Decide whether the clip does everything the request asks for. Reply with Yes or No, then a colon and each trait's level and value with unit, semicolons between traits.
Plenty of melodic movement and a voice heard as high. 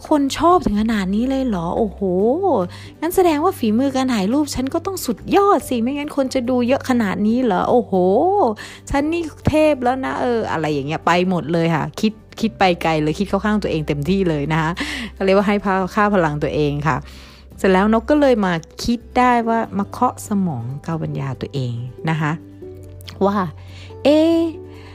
Yes: wide, 8.4 semitones; high, 205 Hz